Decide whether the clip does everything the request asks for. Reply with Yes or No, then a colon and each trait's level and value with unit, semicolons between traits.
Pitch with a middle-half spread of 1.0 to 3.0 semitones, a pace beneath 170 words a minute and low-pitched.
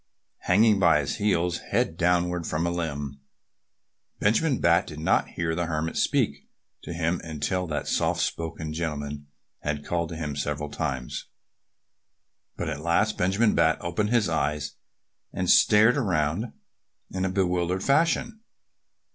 No: average, 3.8 semitones; average, 140 wpm; very low, 85 Hz